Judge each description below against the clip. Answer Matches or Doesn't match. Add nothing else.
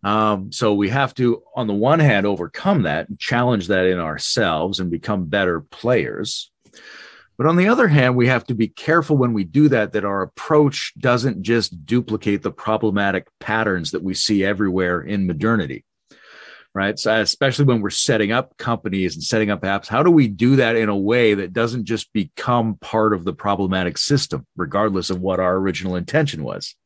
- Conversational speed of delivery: Matches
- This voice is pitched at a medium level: Doesn't match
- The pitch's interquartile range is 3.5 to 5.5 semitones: Matches